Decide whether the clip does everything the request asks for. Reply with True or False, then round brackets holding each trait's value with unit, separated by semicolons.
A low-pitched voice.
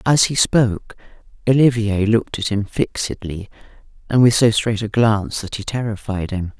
True (110 Hz)